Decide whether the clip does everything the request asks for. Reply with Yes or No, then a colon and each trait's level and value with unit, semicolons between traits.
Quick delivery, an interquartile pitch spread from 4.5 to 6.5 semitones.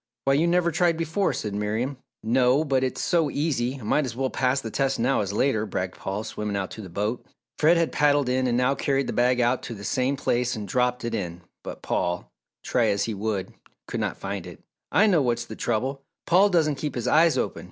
Yes: fast, 230 wpm; average, 4.8 semitones